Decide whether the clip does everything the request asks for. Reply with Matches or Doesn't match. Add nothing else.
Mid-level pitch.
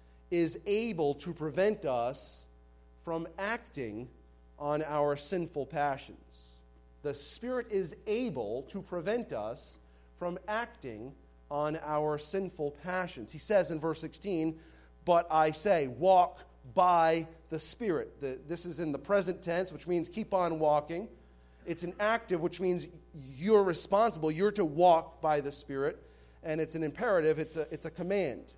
Matches